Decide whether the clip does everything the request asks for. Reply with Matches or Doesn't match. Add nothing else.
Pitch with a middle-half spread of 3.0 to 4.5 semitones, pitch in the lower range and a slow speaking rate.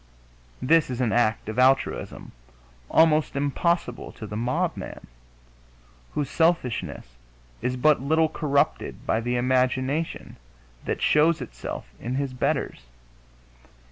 Matches